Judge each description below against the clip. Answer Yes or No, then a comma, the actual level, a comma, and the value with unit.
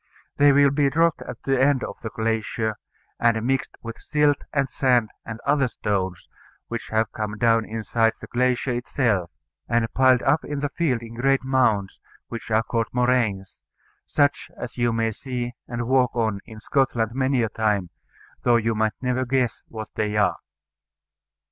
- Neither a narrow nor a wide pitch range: Yes, average, 3.1 semitones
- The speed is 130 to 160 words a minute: No, average, 170 wpm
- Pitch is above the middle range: No, low, 120 Hz